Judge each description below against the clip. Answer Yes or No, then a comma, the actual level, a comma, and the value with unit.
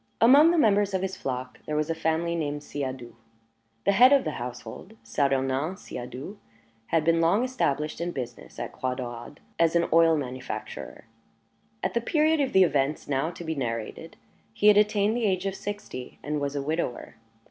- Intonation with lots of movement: Yes, wide, 6.9 semitones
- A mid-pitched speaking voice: Yes, medium, 160 Hz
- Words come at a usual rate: Yes, average, 180 wpm